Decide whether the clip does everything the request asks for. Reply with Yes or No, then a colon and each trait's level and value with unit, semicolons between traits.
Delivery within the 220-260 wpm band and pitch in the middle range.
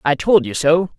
Yes: fast, 245 wpm; medium, 155 Hz